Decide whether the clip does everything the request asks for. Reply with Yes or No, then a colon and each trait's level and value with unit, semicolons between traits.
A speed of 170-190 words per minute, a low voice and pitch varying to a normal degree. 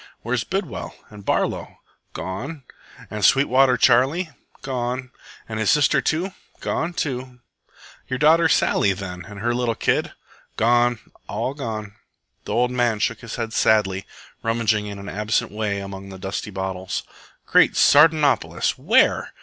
No: slow, 135 wpm; low, 115 Hz; average, 4.1 semitones